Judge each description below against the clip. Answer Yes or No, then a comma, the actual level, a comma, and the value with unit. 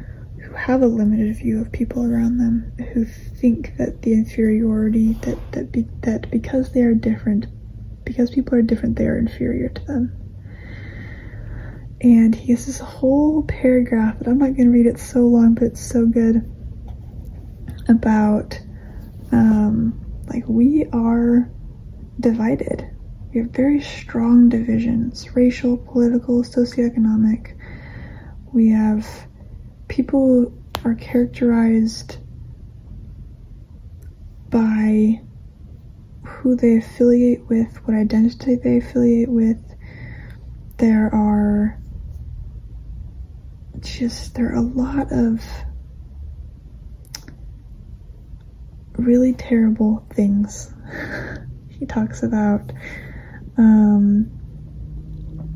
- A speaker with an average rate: No, slow, 100 wpm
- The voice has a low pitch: No, high, 225 Hz